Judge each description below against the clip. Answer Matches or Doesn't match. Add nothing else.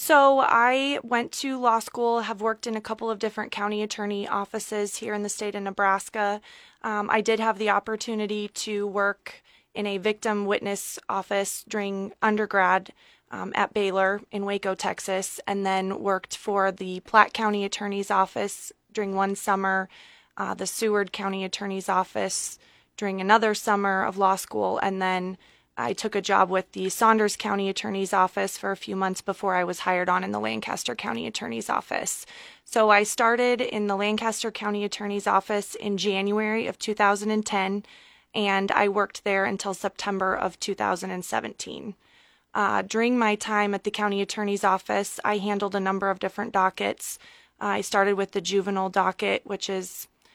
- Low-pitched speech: Doesn't match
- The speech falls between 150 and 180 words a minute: Matches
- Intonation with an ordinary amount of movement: Doesn't match